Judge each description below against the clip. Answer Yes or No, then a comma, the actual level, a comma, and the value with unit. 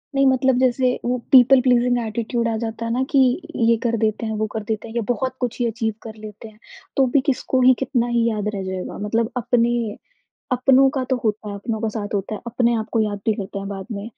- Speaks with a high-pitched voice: Yes, high, 230 Hz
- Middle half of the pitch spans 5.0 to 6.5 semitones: No, narrow, 2.6 semitones